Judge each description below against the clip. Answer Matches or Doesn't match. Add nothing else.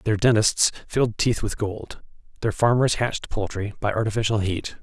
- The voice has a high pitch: Doesn't match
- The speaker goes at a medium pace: Matches